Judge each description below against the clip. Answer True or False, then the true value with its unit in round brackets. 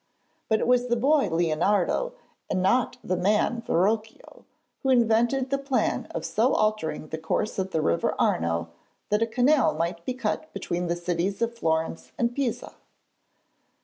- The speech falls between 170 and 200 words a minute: False (160 wpm)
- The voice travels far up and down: True (6.3 semitones)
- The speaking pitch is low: False (215 Hz)